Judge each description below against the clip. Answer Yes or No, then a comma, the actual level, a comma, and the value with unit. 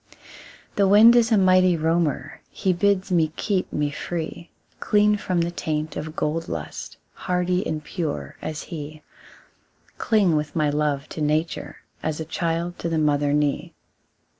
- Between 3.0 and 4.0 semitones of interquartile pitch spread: Yes, average, 3.4 semitones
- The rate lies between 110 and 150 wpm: No, average, 160 wpm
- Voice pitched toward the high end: No, medium, 165 Hz